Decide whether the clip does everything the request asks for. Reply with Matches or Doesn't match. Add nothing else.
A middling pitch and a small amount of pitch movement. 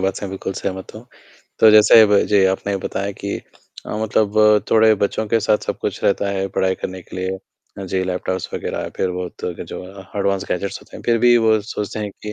Doesn't match